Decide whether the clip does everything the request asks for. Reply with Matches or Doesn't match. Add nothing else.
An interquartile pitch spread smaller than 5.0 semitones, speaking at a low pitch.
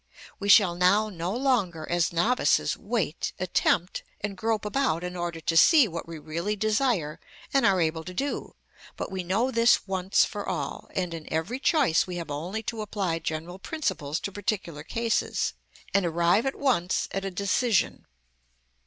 Doesn't match